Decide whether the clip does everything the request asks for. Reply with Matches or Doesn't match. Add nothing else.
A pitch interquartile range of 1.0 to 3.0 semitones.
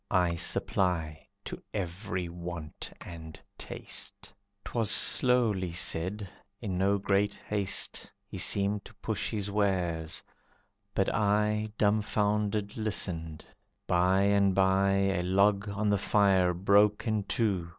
Matches